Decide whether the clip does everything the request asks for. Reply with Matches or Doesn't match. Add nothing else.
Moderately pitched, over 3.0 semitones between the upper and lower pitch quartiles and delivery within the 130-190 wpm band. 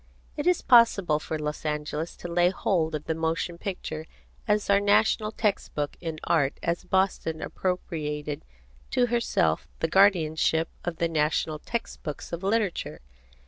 Matches